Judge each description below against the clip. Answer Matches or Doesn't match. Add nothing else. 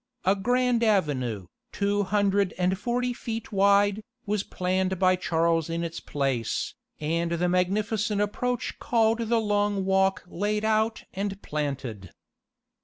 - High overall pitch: Matches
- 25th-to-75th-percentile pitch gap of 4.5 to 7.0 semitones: Doesn't match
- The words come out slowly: Matches